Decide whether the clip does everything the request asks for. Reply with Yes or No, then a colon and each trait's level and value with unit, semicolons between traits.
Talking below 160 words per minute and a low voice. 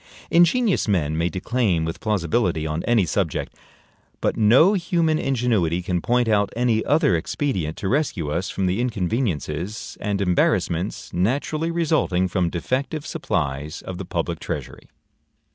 Yes: average, 140 wpm; low, 100 Hz